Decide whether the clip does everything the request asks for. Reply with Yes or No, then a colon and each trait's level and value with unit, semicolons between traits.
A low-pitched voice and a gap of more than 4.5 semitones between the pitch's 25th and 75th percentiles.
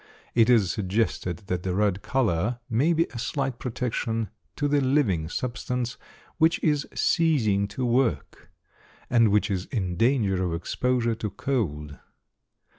Yes: low, 115 Hz; average, 5.0 semitones